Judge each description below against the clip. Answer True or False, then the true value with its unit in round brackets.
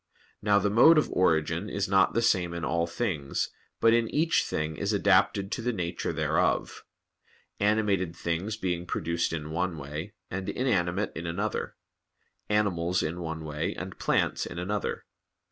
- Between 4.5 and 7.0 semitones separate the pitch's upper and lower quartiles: False (3.8 semitones)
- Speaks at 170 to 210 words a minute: False (160 wpm)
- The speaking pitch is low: True (90 Hz)